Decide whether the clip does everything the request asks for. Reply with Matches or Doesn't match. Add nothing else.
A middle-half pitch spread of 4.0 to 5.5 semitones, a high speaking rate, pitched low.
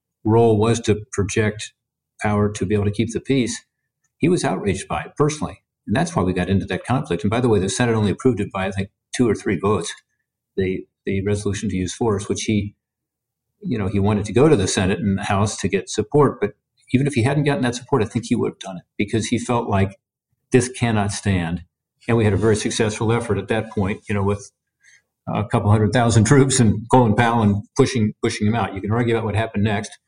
Doesn't match